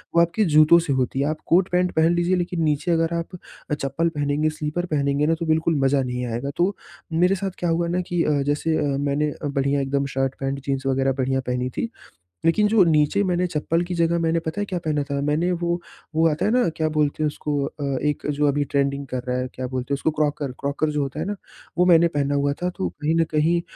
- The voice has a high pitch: No, medium, 150 Hz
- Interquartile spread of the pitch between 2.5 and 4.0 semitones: Yes, average, 3.4 semitones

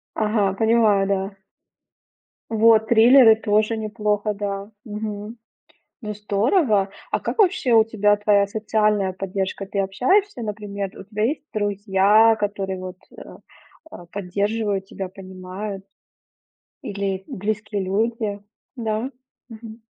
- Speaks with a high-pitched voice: Yes, high, 210 Hz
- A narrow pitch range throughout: Yes, narrow, 1.9 semitones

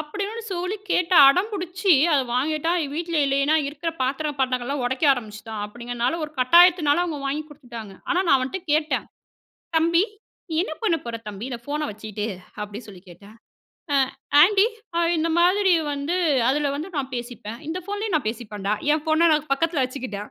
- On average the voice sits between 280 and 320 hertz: Yes, very high, 290 Hz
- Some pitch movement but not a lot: No, wide, 5.8 semitones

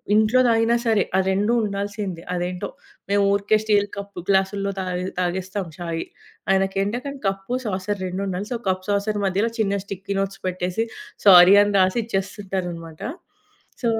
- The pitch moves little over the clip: Yes, narrow, 1.9 semitones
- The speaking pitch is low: No, high, 195 Hz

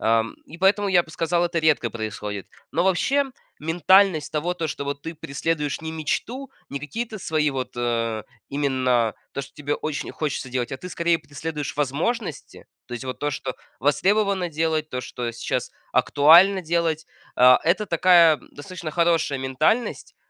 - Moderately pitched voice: Yes, medium, 155 Hz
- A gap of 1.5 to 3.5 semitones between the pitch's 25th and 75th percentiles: No, average, 4.4 semitones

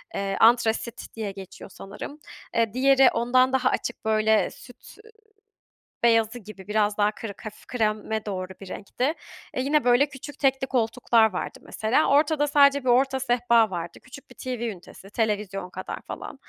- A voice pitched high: Yes, high, 230 Hz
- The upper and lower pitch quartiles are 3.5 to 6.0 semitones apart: Yes, average, 3.9 semitones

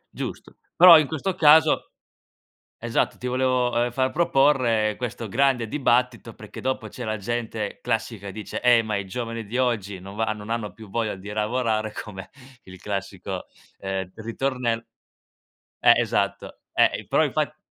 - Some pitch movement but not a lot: Yes, average, 3.3 semitones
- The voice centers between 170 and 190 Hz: No, low, 115 Hz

